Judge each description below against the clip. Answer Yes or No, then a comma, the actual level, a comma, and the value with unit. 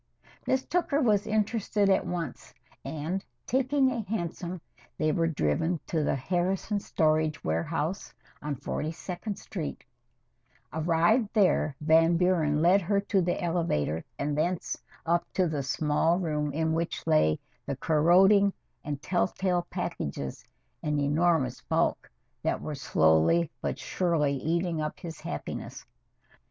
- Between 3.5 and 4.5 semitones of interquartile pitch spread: Yes, average, 3.9 semitones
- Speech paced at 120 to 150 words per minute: Yes, slow, 135 wpm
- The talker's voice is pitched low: No, medium, 165 Hz